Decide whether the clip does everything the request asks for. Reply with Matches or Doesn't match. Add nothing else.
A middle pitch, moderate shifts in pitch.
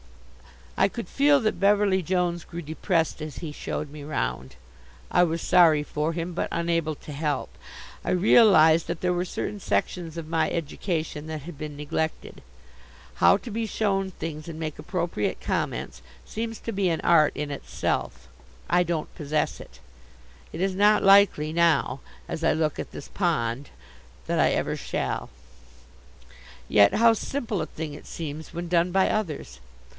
Matches